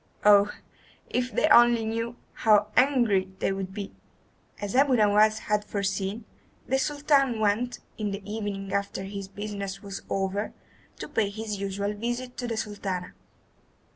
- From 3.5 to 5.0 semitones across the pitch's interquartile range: No, average, 2.8 semitones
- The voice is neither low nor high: No, high, 210 Hz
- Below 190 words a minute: Yes, average, 145 wpm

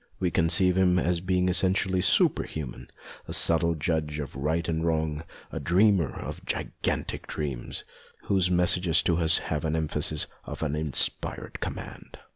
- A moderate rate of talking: Yes, average, 155 wpm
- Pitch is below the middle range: Yes, very low, 80 Hz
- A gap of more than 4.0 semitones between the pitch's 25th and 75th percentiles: No, average, 2.8 semitones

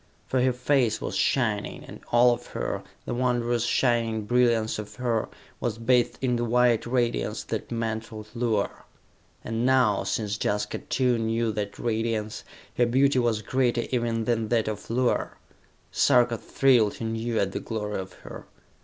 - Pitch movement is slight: Yes, narrow, 1.9 semitones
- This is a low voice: Yes, low, 115 Hz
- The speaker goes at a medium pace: Yes, average, 155 wpm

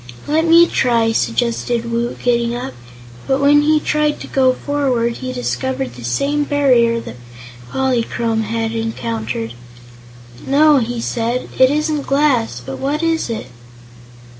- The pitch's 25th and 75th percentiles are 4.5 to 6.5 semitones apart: No, average, 3.9 semitones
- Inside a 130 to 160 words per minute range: Yes, average, 140 wpm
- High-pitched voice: Yes, very high, 250 Hz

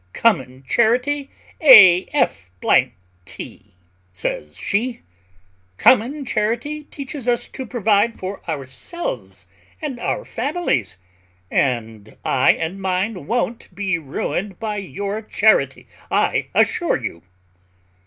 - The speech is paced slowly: Yes, slow, 105 wpm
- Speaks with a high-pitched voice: Yes, high, 210 Hz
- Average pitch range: No, wide, 7.6 semitones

